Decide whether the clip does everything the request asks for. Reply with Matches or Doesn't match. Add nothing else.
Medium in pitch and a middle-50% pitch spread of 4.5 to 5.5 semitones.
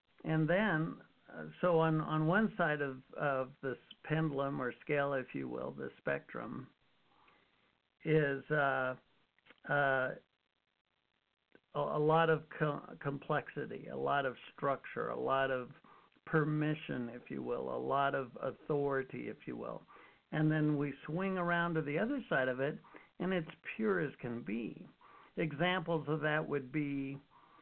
Doesn't match